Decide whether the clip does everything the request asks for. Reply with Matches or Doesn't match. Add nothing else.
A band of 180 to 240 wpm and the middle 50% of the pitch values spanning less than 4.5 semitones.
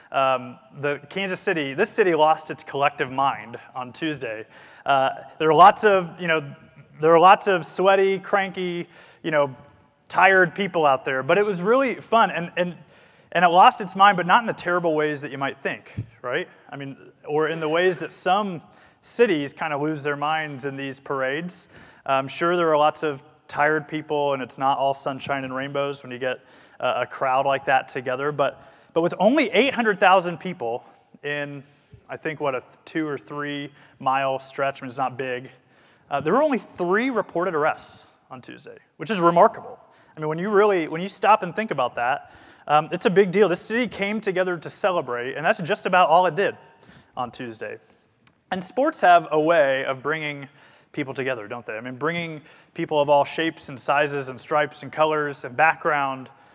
Doesn't match